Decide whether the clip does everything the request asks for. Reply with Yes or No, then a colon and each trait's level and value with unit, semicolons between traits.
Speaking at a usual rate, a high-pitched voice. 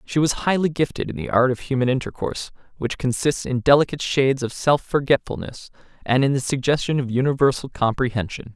No: average, 175 wpm; low, 135 Hz